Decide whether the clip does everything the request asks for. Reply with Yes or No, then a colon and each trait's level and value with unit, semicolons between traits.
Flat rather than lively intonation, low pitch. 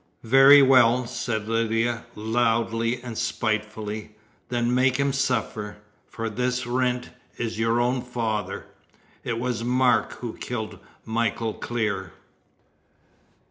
Yes: narrow, 2.0 semitones; low, 115 Hz